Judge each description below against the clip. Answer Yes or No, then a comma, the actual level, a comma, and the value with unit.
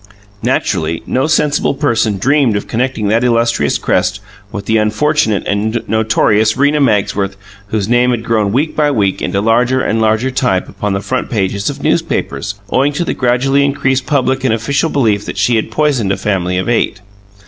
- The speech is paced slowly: No, average, 180 wpm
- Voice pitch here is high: No, low, 115 Hz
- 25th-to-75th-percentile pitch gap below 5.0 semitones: Yes, average, 4.4 semitones